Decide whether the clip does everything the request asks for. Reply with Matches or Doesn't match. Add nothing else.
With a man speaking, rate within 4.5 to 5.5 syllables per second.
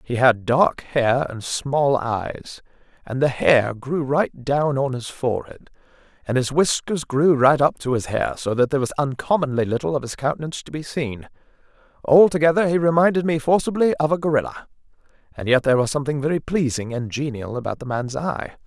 Matches